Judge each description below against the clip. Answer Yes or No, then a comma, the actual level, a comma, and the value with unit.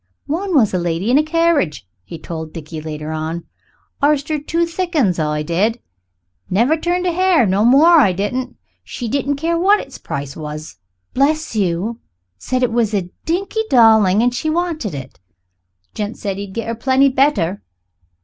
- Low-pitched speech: No, high, 235 Hz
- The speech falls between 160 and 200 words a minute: Yes, average, 175 wpm